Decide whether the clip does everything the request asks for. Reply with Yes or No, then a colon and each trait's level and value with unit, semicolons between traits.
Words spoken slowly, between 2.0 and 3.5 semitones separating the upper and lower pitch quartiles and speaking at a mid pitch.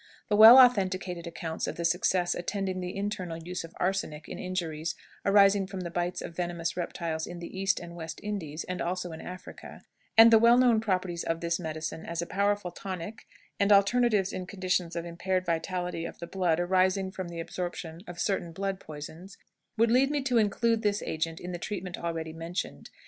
No: average, 190 wpm; average, 2.8 semitones; medium, 180 Hz